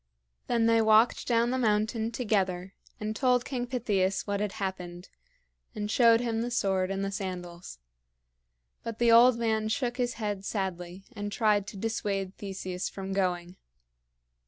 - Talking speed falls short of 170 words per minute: Yes, average, 155 wpm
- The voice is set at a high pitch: Yes, high, 210 Hz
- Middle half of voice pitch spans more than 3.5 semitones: No, average, 3.2 semitones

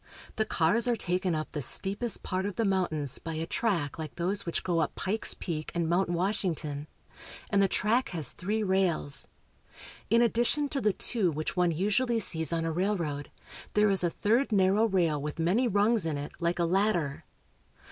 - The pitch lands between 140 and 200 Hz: Yes, medium, 185 Hz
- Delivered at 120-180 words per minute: No, average, 190 wpm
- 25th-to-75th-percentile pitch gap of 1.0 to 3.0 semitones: No, average, 4.4 semitones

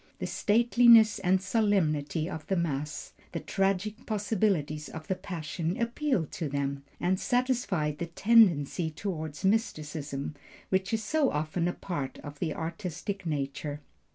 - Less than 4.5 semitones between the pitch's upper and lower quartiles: No, wide, 5.4 semitones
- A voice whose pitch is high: No, medium, 175 Hz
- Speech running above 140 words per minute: No, slow, 135 wpm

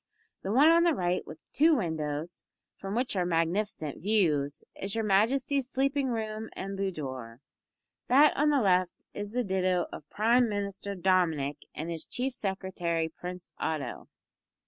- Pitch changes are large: Yes, wide, 5.7 semitones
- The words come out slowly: No, average, 150 wpm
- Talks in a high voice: Yes, high, 195 Hz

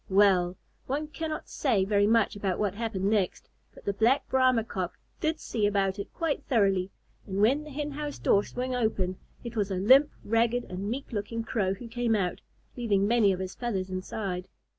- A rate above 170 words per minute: Yes, average, 190 wpm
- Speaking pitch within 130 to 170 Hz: No, high, 215 Hz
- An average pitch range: Yes, average, 4.1 semitones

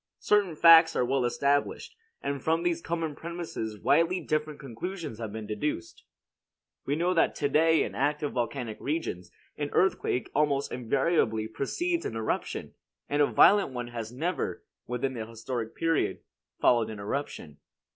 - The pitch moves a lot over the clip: Yes, wide, 5.8 semitones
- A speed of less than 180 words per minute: Yes, average, 150 wpm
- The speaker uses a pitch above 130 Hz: Yes, medium, 140 Hz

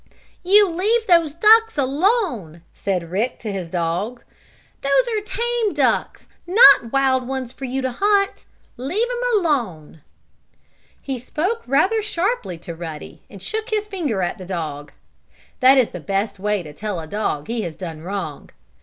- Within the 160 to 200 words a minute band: Yes, average, 165 wpm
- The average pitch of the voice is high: Yes, very high, 260 Hz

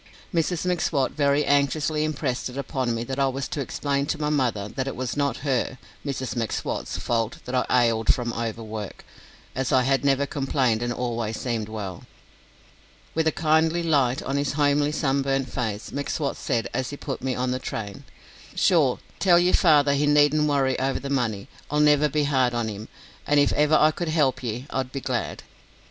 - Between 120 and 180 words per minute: No, average, 190 wpm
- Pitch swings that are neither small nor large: Yes, average, 3.2 semitones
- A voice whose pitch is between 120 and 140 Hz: Yes, low, 135 Hz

